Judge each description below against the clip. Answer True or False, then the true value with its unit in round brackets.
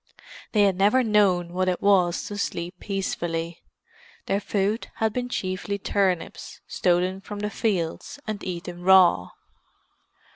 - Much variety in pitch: False (2.5 semitones)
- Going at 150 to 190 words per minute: False (135 wpm)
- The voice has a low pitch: False (190 Hz)